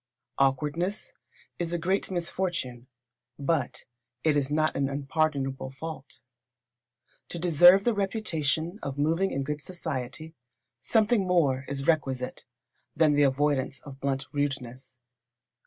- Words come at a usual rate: No, slow, 120 wpm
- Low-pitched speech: No, medium, 150 Hz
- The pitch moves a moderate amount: Yes, average, 4.1 semitones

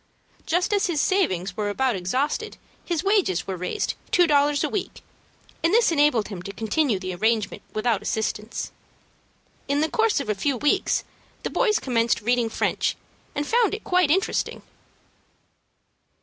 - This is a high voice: Yes, very high, 280 Hz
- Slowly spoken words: No, average, 155 wpm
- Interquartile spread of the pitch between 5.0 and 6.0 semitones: No, wide, 8.8 semitones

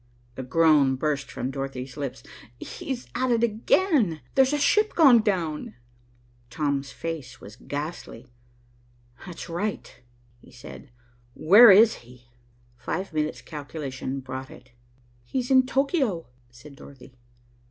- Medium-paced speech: No, slow, 120 wpm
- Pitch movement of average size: No, wide, 9.0 semitones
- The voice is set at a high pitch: No, medium, 155 Hz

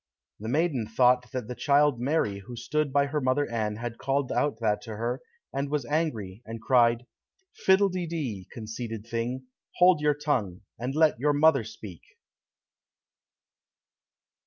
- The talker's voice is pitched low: Yes, low, 125 Hz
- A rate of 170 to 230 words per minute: No, average, 155 wpm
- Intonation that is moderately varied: Yes, average, 4.5 semitones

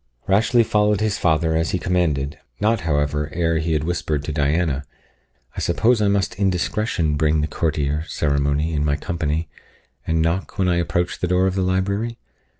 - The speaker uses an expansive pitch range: No, average, 3.8 semitones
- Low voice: Yes, very low, 85 Hz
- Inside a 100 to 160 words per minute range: No, average, 180 wpm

